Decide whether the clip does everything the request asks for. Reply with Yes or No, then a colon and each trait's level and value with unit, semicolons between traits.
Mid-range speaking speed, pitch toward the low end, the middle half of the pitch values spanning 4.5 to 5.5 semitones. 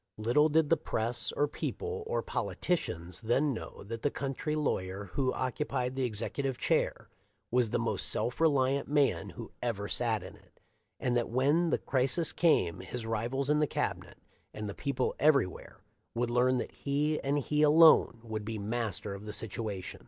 Yes: average, 175 wpm; low, 125 Hz; average, 4.8 semitones